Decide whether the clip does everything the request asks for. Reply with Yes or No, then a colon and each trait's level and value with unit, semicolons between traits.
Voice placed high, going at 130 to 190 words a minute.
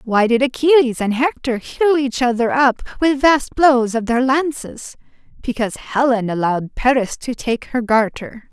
Yes: very high, 250 Hz; average, 160 wpm